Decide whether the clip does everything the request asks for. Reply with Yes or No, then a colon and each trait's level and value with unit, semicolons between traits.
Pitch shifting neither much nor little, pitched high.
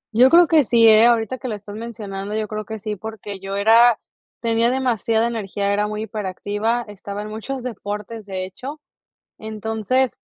No: narrow, 2.3 semitones; high, 220 Hz